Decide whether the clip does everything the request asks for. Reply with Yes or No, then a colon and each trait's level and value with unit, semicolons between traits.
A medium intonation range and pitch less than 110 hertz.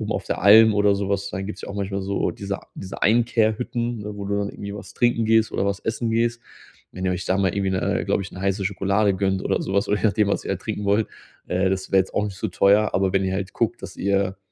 No: narrow, 1.7 semitones; low, 100 Hz